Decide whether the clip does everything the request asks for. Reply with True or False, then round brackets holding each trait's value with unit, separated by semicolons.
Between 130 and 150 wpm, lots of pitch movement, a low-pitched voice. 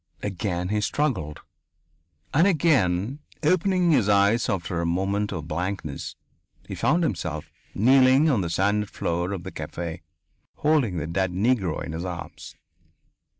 True (140 wpm; 7.1 semitones; 100 Hz)